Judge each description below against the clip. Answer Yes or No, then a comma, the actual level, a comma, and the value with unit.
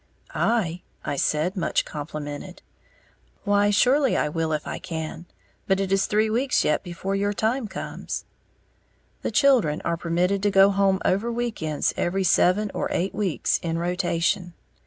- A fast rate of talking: No, average, 155 wpm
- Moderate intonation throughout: Yes, average, 3.7 semitones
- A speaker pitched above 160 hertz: Yes, high, 190 Hz